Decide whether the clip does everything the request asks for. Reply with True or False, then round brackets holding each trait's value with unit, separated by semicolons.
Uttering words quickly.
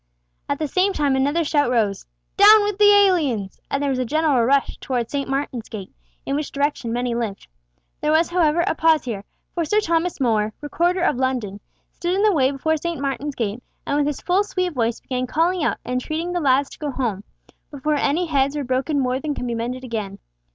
True (215 wpm)